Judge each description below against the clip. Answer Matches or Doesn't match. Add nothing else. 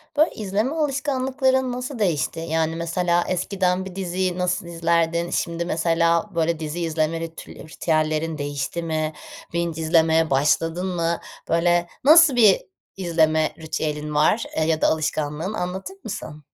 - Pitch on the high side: Doesn't match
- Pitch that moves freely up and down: Doesn't match